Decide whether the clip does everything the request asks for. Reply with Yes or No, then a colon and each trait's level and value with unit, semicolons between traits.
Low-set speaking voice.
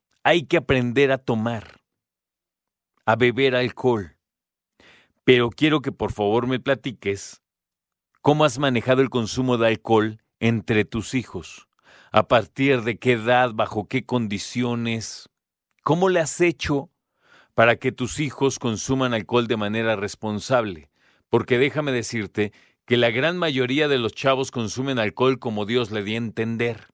Yes: low, 120 Hz